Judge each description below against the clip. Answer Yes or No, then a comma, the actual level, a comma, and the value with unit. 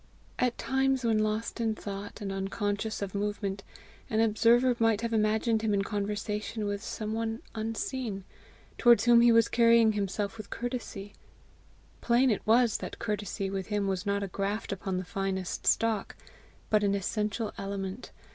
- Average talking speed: Yes, average, 160 wpm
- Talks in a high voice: Yes, high, 215 Hz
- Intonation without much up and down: Yes, narrow, 2.3 semitones